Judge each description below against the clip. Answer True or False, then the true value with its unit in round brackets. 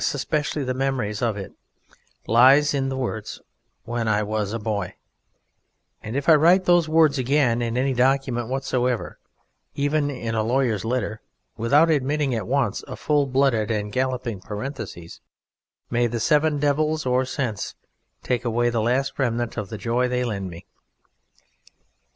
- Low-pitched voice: True (125 Hz)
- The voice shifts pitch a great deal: False (3.6 semitones)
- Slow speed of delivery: False (155 wpm)